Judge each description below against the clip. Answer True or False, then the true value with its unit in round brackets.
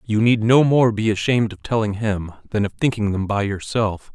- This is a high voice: False (110 Hz)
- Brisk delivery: True (215 wpm)